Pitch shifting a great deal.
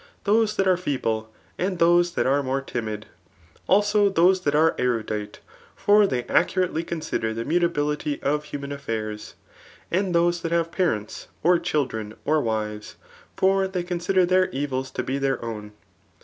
Yes: wide, 6.7 semitones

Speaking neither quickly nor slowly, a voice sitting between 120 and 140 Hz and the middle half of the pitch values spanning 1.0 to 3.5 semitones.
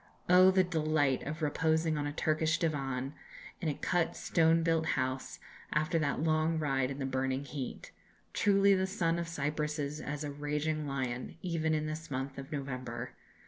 No: average, 175 wpm; medium, 150 Hz; average, 2.8 semitones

